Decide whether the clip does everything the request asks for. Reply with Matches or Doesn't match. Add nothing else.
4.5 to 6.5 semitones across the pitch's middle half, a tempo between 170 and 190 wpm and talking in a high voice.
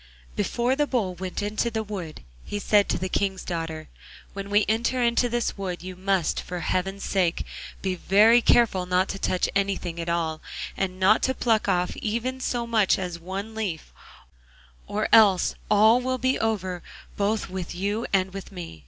Doesn't match